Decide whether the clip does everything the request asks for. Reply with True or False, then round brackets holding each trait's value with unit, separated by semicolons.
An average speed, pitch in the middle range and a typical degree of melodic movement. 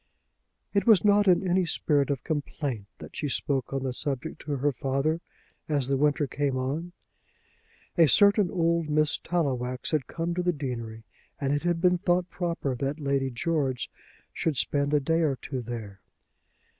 True (170 wpm; 145 Hz; 4.0 semitones)